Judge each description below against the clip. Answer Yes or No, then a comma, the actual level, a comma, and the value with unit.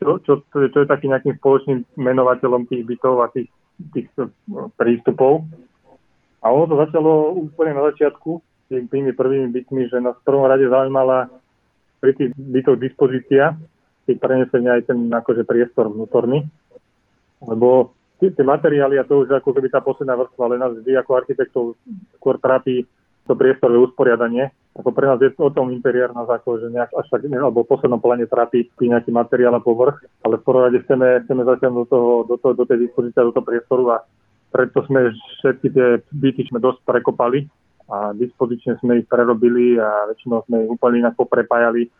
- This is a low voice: Yes, low, 125 Hz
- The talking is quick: Yes, fast, 170 wpm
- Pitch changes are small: Yes, narrow, 2.0 semitones